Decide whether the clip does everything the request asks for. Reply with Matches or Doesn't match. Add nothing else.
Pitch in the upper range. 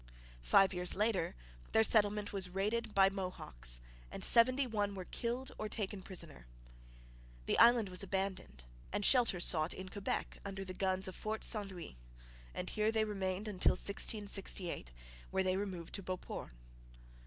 Matches